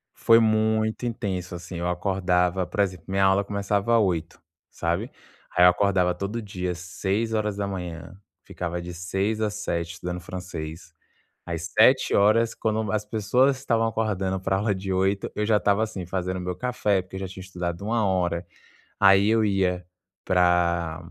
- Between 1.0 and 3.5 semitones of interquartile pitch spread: Yes, average, 3.0 semitones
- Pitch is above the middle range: No, very low, 95 Hz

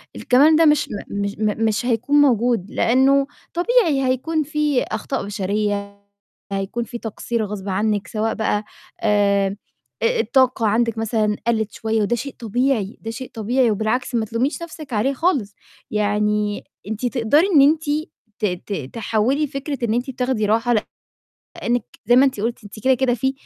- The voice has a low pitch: No, high, 230 Hz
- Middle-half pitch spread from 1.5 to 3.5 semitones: No, average, 4.0 semitones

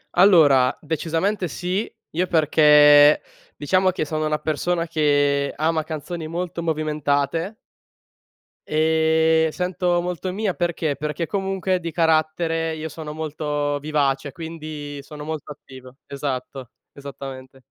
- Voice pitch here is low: No, medium, 155 Hz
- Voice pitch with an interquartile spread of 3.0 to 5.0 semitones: No, narrow, 2.5 semitones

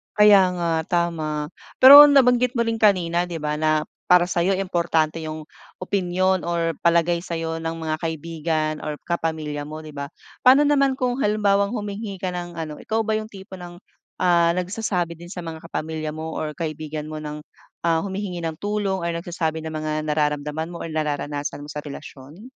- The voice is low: No, medium, 170 Hz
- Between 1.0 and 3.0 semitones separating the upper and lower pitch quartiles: No, average, 3.7 semitones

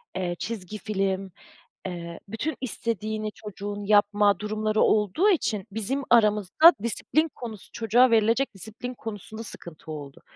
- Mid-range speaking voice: No, high, 215 Hz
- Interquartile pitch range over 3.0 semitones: No, average, 2.7 semitones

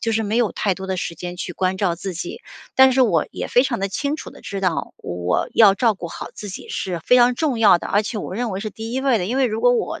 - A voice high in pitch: Yes, high, 210 Hz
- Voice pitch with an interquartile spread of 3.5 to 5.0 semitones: Yes, average, 4.6 semitones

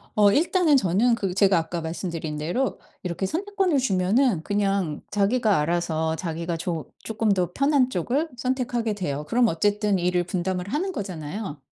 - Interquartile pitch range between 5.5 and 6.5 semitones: Yes, wide, 6.2 semitones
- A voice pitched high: Yes, high, 195 Hz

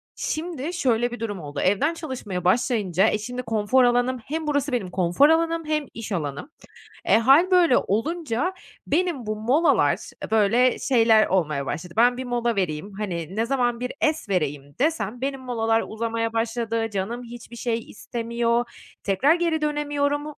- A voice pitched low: No, high, 235 Hz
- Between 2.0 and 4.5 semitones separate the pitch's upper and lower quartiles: No, average, 5.2 semitones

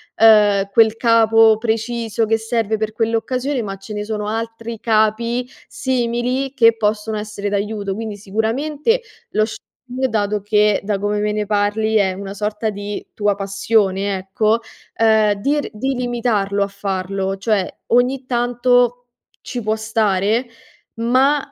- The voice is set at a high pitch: Yes, high, 220 Hz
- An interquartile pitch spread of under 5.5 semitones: Yes, narrow, 2.4 semitones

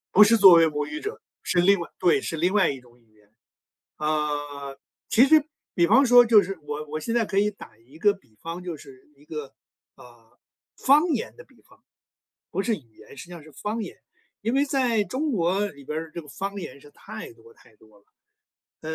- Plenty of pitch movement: Yes, wide, 6.9 semitones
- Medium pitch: Yes, medium, 170 Hz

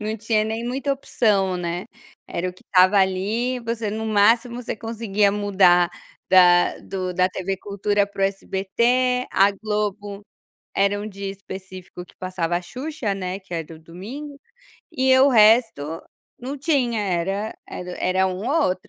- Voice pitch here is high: Yes, high, 200 Hz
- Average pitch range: Yes, average, 3.7 semitones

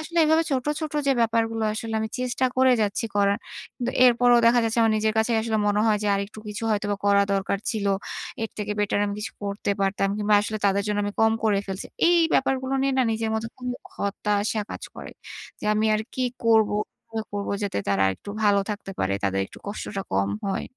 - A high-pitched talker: Yes, high, 215 Hz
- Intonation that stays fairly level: Yes, narrow, 2.3 semitones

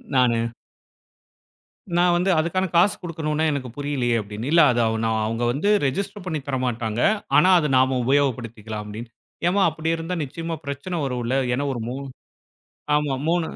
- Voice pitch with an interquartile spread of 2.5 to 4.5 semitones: No, average, 5.3 semitones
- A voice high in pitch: No, medium, 140 Hz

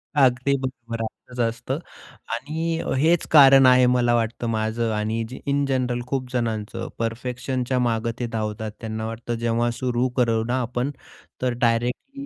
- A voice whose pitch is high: No, low, 120 Hz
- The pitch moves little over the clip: Yes, narrow, 2.2 semitones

